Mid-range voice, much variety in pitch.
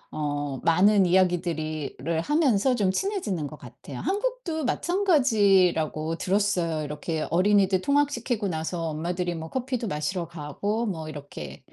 Yes: medium, 180 Hz; wide, 6.1 semitones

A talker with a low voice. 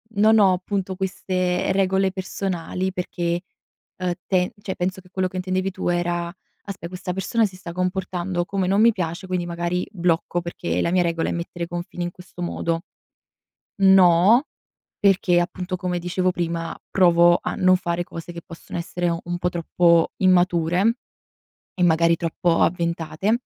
No: medium, 180 Hz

